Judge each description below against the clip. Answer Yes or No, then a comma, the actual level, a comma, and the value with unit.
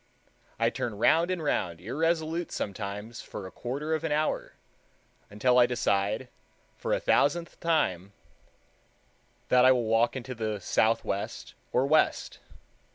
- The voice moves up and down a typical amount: No, wide, 6.7 semitones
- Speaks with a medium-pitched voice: No, low, 125 Hz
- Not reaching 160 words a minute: Yes, slow, 135 wpm